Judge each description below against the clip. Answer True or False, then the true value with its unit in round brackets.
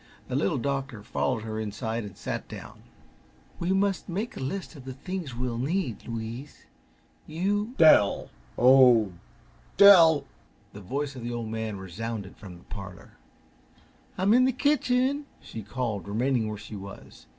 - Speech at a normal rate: True (160 wpm)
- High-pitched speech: False (125 Hz)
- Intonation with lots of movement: True (8.5 semitones)